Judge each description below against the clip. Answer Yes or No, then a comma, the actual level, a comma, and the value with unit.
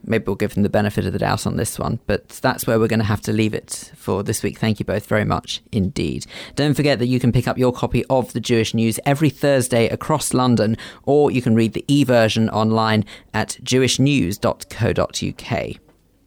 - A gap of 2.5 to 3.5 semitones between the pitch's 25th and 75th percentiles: Yes, average, 2.9 semitones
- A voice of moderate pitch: No, low, 115 Hz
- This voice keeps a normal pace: No, fast, 210 wpm